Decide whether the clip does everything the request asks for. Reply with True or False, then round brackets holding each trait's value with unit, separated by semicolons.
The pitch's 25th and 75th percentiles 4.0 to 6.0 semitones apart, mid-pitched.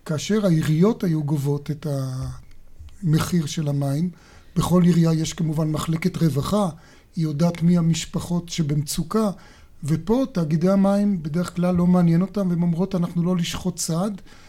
False (2.6 semitones; 170 Hz)